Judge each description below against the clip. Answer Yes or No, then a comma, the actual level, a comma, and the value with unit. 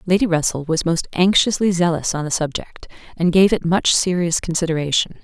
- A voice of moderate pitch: Yes, medium, 170 Hz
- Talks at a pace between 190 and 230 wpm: No, average, 170 wpm